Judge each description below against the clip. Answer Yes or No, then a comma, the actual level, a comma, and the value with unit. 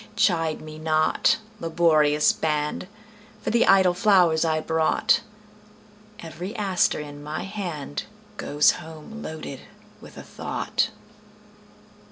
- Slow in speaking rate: Yes, slow, 95 wpm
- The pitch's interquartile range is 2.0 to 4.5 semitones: No, average, 5.1 semitones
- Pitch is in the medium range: Yes, medium, 170 Hz